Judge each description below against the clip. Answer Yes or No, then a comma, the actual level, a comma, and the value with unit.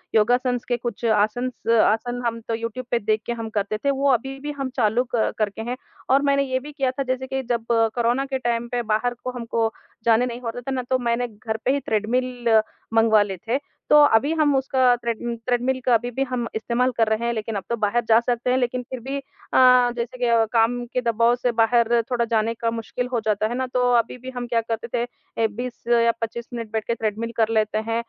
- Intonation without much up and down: Yes, narrow, 1.9 semitones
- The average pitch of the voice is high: Yes, high, 235 Hz